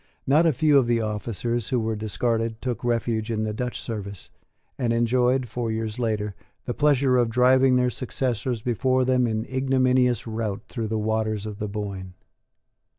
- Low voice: Yes, low, 115 Hz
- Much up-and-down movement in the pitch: No, average, 2.7 semitones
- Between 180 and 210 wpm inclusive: No, average, 170 wpm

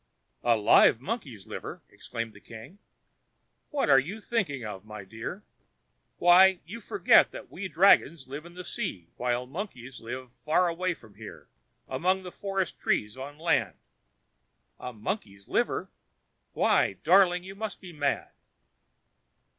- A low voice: No, medium, 150 Hz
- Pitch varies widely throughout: Yes, wide, 8.0 semitones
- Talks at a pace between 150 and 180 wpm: No, average, 140 wpm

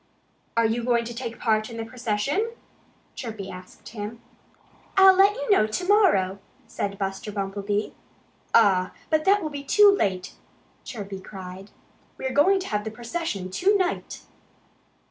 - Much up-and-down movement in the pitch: Yes, wide, 8.5 semitones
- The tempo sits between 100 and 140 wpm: No, average, 150 wpm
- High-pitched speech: Yes, high, 230 Hz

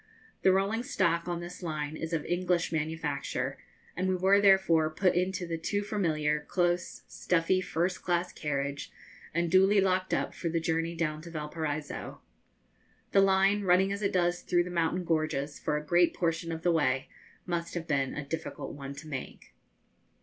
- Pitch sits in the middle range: Yes, medium, 170 Hz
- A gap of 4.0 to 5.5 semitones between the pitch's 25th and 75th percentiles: No, average, 2.9 semitones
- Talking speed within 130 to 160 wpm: No, average, 170 wpm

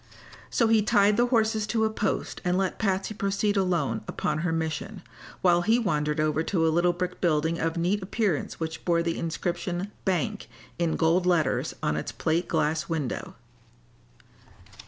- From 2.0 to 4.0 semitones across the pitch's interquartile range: Yes, average, 3.7 semitones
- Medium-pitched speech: Yes, medium, 175 Hz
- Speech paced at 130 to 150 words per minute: No, average, 165 wpm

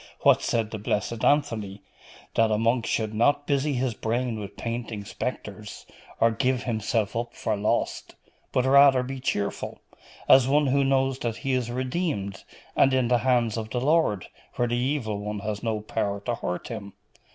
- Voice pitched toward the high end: No, low, 120 Hz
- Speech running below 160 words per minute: No, average, 175 wpm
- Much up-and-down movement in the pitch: No, average, 3.5 semitones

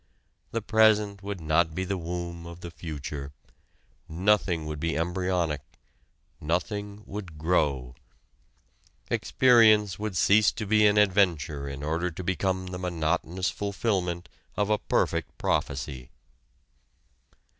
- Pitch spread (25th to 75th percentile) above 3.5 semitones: Yes, average, 4.2 semitones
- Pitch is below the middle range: Yes, very low, 90 Hz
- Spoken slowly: Yes, slow, 120 wpm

